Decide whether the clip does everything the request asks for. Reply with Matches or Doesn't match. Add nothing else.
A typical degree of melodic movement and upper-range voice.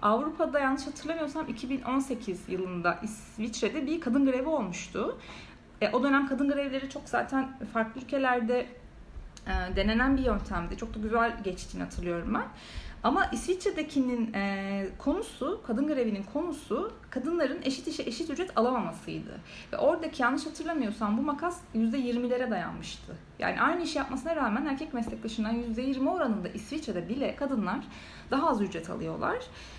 Matches